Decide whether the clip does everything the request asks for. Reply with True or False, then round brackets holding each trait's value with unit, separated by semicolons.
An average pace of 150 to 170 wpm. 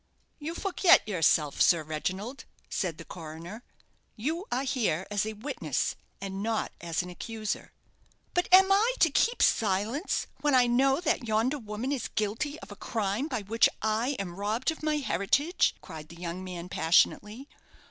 True (165 wpm)